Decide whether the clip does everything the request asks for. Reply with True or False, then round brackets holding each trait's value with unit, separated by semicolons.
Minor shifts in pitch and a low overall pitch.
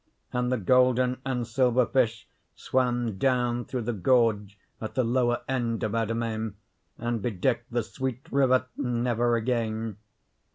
True (2.0 semitones; 120 Hz)